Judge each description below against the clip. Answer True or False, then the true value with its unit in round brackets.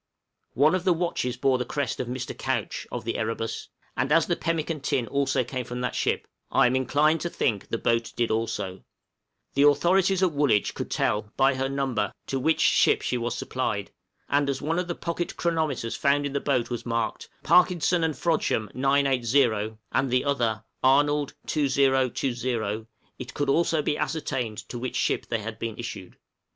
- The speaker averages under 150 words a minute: False (185 wpm)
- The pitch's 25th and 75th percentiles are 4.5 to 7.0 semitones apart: False (4.0 semitones)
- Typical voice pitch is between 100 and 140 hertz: True (135 Hz)